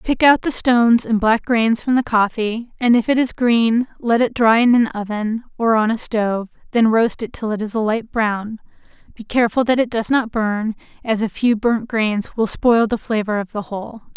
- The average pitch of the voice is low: No, high, 225 Hz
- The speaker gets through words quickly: Yes, fast, 225 wpm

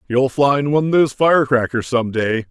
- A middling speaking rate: Yes, average, 190 wpm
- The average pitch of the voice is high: No, low, 130 Hz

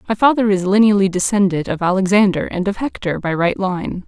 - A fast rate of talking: No, average, 190 wpm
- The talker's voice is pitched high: Yes, high, 195 Hz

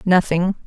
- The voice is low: No, medium, 180 Hz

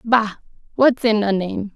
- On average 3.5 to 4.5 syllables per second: Yes, 4.2 syllables/s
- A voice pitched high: Yes, high, 215 Hz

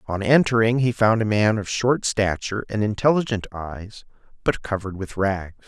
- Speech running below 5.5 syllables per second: Yes, 5.1 syllables/s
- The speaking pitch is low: Yes, low, 105 Hz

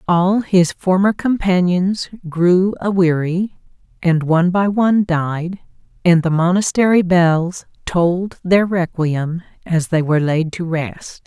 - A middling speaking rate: No, slow, 130 wpm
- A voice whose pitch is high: No, medium, 175 Hz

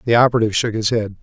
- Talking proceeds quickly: Yes, fast, 245 wpm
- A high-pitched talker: No, low, 110 Hz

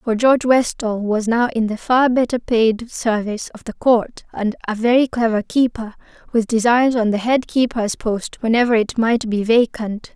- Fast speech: No, average, 175 wpm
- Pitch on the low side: No, high, 230 Hz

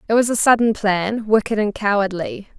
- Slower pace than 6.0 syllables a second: Yes, 5.1 syllables/s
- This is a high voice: Yes, high, 210 Hz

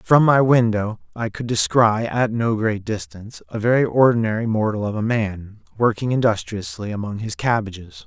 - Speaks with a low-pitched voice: Yes, low, 110 Hz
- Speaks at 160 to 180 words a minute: Yes, average, 165 wpm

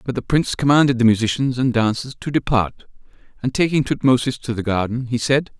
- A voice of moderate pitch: No, low, 125 Hz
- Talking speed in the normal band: Yes, average, 195 wpm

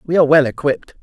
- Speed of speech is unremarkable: No, fast, 235 wpm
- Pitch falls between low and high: Yes, medium, 150 Hz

